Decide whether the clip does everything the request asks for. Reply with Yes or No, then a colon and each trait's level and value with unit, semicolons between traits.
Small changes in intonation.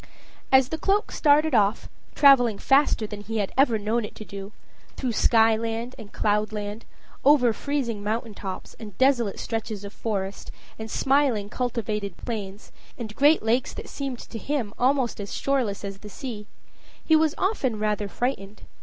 No: average, 4.2 semitones